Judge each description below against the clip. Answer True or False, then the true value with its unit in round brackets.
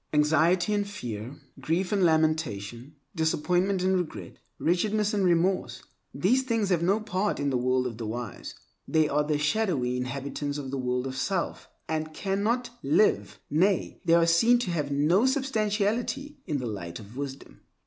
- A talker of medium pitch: True (165 Hz)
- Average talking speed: True (160 wpm)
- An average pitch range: False (6.5 semitones)